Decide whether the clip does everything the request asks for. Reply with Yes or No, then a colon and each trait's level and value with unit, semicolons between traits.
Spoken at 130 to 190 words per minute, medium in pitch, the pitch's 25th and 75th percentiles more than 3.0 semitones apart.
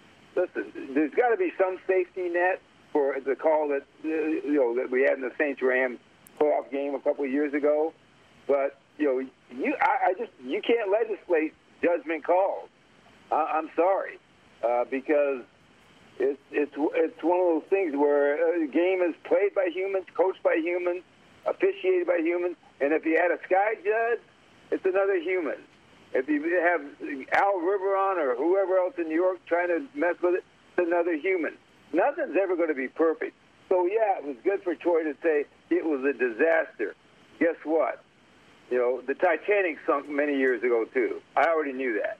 Yes: average, 180 wpm; medium, 175 Hz; average, 4.9 semitones